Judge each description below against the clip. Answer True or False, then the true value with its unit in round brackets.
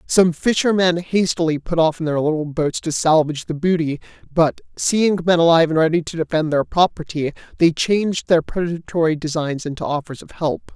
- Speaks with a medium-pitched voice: True (165 Hz)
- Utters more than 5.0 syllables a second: True (5.4 syllables/s)